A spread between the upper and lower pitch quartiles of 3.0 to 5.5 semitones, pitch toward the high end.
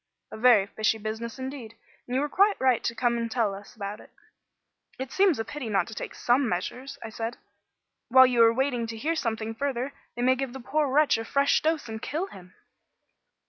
Yes: average, 3.4 semitones; high, 245 Hz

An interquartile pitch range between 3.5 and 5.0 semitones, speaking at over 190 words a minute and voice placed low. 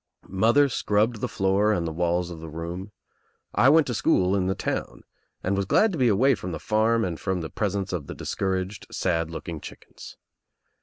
Yes: average, 3.9 semitones; average, 200 wpm; very low, 95 Hz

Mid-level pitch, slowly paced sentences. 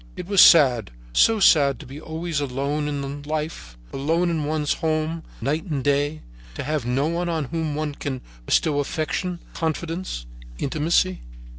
No: medium, 155 Hz; average, 155 wpm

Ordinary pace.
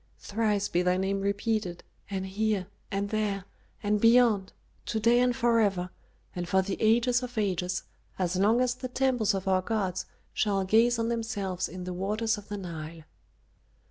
Yes: average, 170 wpm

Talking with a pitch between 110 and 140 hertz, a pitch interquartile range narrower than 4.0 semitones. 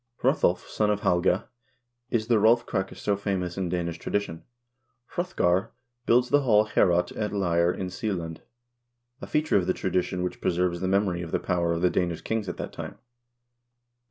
No: very low, 95 Hz; average, 3.3 semitones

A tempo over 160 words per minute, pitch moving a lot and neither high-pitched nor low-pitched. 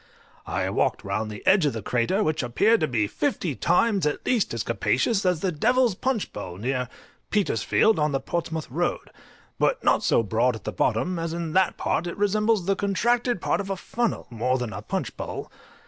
Yes: average, 200 wpm; wide, 9.0 semitones; medium, 165 Hz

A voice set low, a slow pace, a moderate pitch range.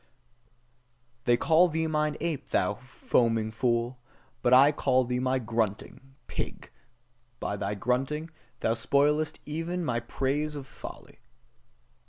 Yes: low, 130 Hz; slow, 125 wpm; average, 4.4 semitones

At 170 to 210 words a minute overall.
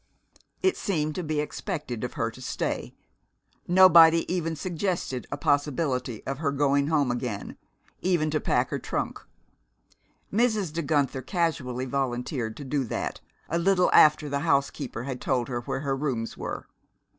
No: average, 155 wpm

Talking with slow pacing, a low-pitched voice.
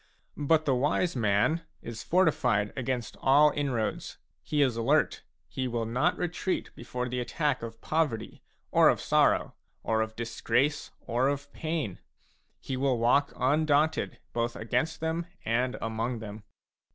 No: average, 145 wpm; low, 125 Hz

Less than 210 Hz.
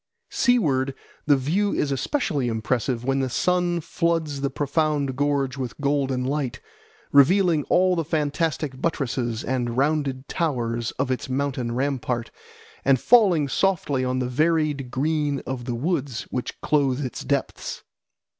Yes: medium, 140 Hz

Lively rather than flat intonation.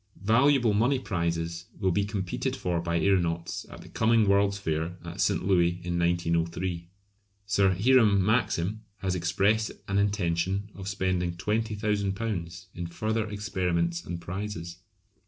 No: average, 3.5 semitones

